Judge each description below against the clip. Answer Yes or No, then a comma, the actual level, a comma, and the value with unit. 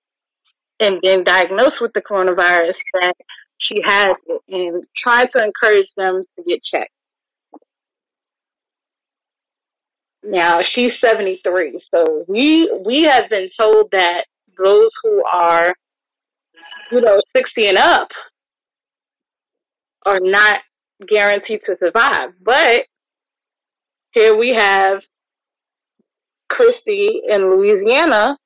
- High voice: Yes, high, 215 Hz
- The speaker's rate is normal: No, slow, 100 wpm